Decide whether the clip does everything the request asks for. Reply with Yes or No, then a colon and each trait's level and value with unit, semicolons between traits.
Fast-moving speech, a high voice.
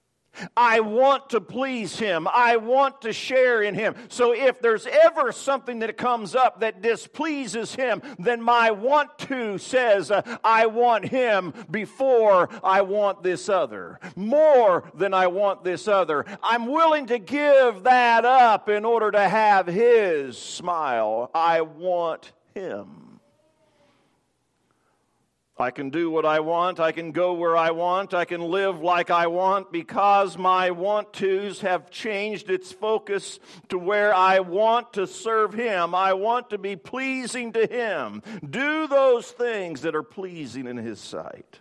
No: average, 155 wpm; high, 210 Hz